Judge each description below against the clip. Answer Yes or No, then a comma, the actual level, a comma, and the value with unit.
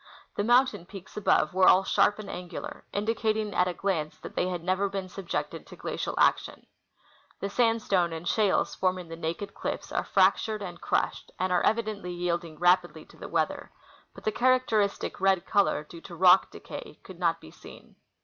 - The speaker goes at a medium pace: Yes, average, 185 wpm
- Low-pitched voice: No, high, 190 Hz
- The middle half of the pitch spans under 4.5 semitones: Yes, average, 2.9 semitones